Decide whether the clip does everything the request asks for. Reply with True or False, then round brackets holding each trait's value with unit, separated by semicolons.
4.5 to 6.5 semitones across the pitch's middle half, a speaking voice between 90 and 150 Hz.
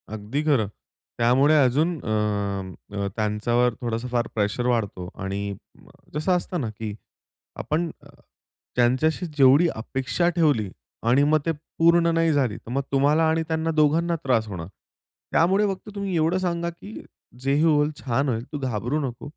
True (5.5 semitones; 140 Hz)